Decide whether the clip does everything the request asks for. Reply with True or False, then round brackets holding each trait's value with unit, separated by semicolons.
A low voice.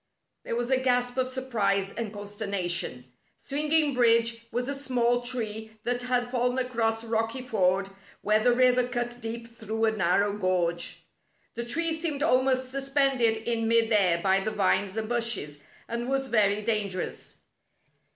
False (230 Hz)